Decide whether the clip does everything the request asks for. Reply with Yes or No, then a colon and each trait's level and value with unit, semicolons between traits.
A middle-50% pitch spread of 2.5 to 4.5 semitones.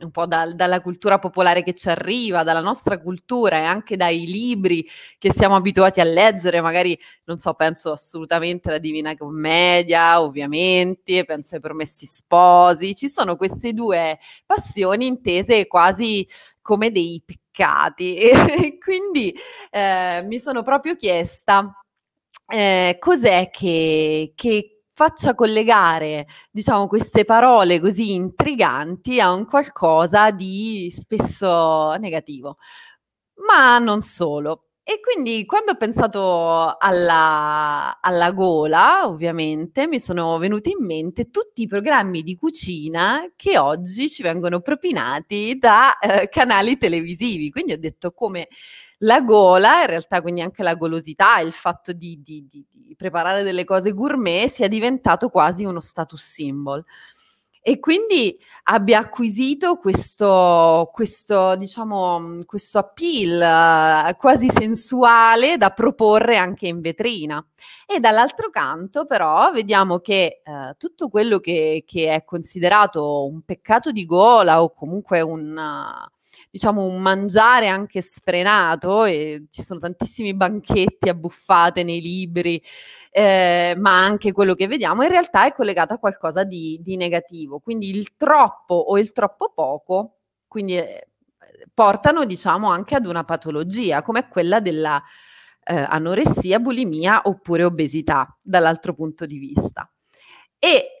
No: average, 5.2 semitones